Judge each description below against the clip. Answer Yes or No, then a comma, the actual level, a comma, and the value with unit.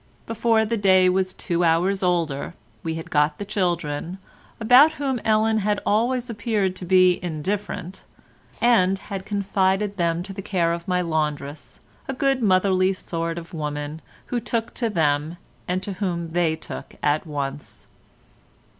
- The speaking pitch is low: No, medium, 185 Hz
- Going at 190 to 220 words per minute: No, average, 155 wpm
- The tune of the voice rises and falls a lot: No, average, 4.0 semitones